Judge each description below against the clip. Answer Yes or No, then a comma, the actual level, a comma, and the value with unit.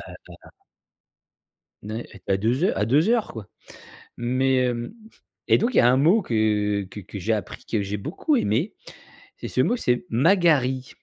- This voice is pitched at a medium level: No, low, 120 Hz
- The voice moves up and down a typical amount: No, wide, 6.4 semitones